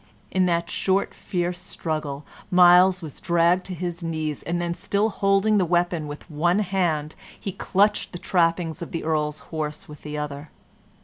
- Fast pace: No, average, 170 wpm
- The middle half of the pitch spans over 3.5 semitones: No, average, 2.9 semitones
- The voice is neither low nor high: Yes, medium, 170 Hz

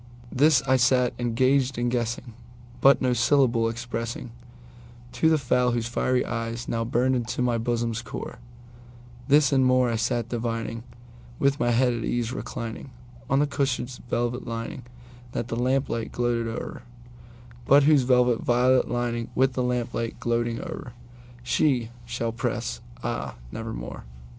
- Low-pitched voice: Yes, low, 120 Hz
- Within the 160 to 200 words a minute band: No, slow, 135 wpm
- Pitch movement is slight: Yes, narrow, 1.4 semitones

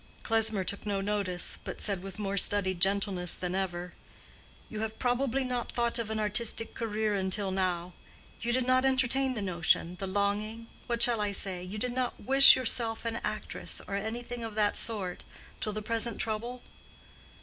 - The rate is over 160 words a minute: Yes, average, 170 wpm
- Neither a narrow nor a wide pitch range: Yes, average, 3.3 semitones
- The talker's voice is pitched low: No, high, 215 Hz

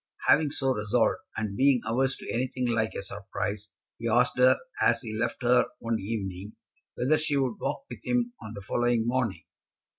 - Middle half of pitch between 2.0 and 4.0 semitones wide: Yes, average, 3.3 semitones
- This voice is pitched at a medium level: No, low, 115 Hz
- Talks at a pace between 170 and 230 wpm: Yes, average, 180 wpm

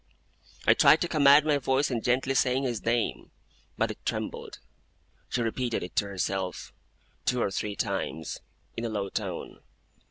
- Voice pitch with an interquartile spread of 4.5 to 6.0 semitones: Yes, average, 4.9 semitones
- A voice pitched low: Yes, low, 120 Hz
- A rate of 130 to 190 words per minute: Yes, average, 160 wpm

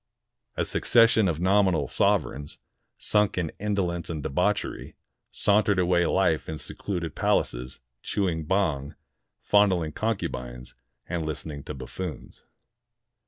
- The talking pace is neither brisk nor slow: No, slow, 110 wpm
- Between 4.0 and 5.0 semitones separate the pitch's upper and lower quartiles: Yes, average, 4.7 semitones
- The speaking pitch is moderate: No, very low, 85 Hz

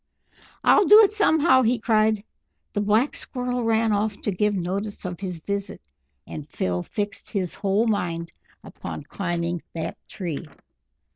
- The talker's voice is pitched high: Yes, high, 205 Hz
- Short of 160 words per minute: Yes, average, 145 wpm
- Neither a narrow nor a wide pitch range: Yes, average, 4.2 semitones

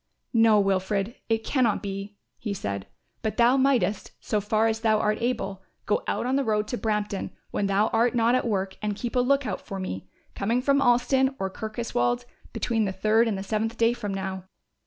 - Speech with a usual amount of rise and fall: Yes, average, 3.2 semitones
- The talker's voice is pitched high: Yes, high, 215 Hz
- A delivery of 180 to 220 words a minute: Yes, average, 200 wpm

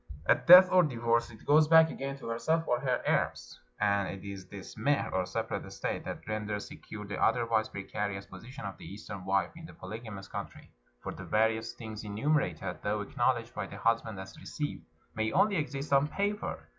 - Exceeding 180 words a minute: Yes, average, 195 wpm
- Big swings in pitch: Yes, wide, 5.8 semitones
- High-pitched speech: No, low, 110 Hz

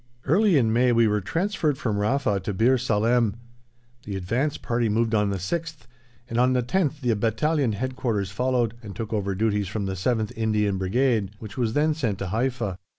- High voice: No, low, 115 Hz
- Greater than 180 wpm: Yes, average, 195 wpm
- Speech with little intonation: No, average, 3.9 semitones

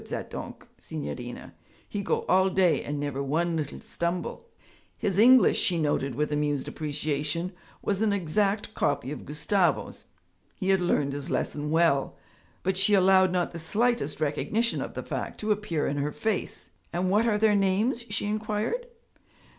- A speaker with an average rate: Yes, average, 160 wpm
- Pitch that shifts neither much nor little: No, wide, 5.7 semitones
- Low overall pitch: No, medium, 180 Hz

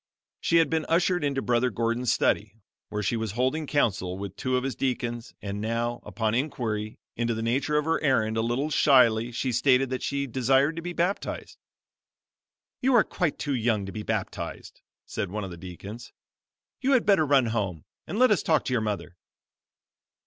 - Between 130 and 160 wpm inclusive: No, average, 190 wpm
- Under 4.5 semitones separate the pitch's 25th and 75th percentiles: No, average, 4.8 semitones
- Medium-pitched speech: No, low, 120 Hz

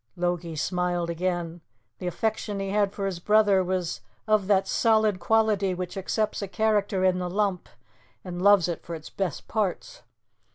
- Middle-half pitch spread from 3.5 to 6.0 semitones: No, average, 2.8 semitones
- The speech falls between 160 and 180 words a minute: Yes, average, 165 wpm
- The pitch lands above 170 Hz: Yes, high, 190 Hz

